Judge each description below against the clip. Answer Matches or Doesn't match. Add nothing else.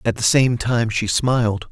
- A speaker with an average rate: Doesn't match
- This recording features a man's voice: Matches